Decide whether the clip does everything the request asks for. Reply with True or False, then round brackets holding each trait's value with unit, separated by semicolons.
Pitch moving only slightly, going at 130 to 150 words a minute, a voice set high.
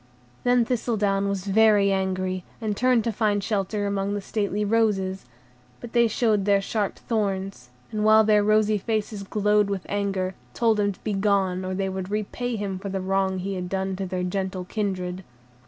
False (2.0 semitones; 175 wpm; 200 Hz)